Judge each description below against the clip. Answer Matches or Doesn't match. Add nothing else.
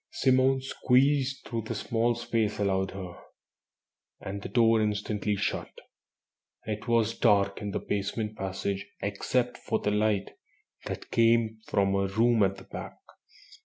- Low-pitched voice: Matches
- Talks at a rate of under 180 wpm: Matches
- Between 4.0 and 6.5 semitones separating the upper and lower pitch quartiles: Doesn't match